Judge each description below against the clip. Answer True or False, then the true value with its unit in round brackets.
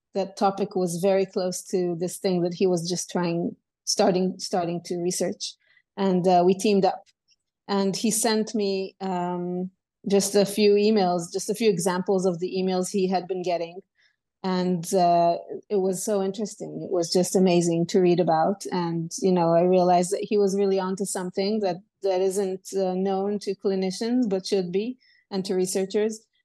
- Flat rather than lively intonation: True (1.8 semitones)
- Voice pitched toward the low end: False (190 Hz)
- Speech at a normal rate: True (180 wpm)